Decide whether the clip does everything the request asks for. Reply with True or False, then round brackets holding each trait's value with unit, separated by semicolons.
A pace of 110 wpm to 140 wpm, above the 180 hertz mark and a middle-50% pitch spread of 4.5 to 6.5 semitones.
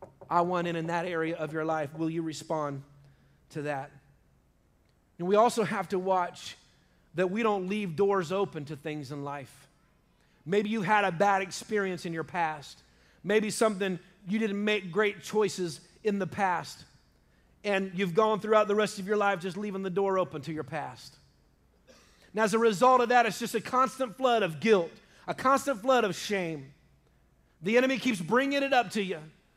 False (185 wpm; 190 Hz; 5.1 semitones)